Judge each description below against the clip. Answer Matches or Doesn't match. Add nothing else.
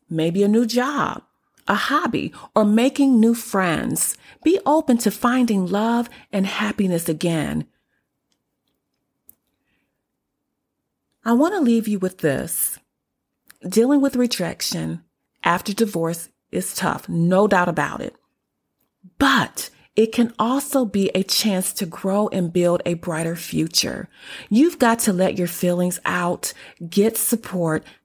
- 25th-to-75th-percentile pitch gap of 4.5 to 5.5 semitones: Matches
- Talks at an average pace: Doesn't match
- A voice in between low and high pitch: Doesn't match